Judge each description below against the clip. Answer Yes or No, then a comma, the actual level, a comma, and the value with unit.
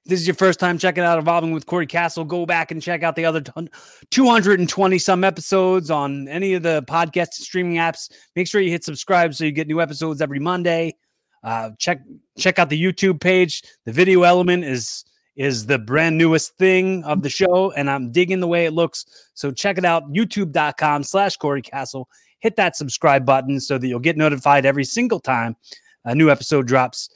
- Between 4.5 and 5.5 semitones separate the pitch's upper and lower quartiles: No, average, 4.0 semitones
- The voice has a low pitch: No, medium, 165 Hz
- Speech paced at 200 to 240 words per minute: Yes, fast, 205 wpm